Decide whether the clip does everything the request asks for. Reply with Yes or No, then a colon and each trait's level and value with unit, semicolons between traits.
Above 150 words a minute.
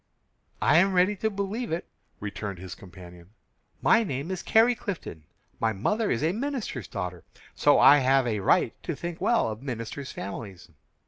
Yes: average, 170 wpm